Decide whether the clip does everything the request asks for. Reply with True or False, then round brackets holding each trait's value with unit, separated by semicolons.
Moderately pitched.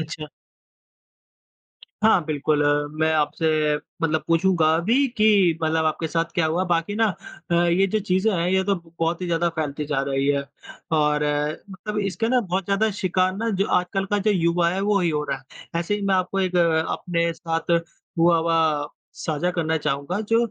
True (170 Hz)